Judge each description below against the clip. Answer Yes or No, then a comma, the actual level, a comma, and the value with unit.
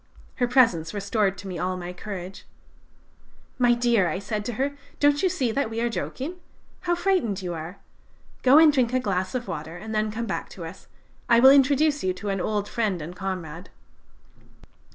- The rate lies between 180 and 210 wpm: Yes, average, 195 wpm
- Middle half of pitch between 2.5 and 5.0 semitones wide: No, wide, 5.6 semitones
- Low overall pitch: No, high, 215 Hz